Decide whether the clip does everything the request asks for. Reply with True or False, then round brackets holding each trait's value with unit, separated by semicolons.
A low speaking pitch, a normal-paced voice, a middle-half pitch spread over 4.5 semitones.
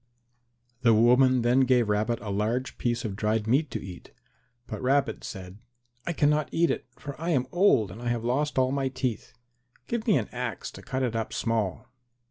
False (120 Hz; 195 wpm; 3.4 semitones)